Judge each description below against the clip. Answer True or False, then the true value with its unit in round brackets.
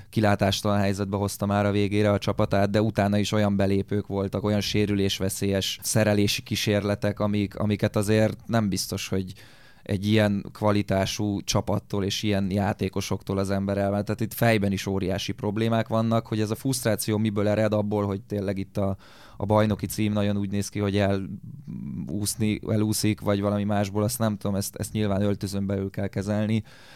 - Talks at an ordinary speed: False (165 wpm)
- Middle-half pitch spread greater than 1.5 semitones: False (1.2 semitones)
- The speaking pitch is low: True (105 Hz)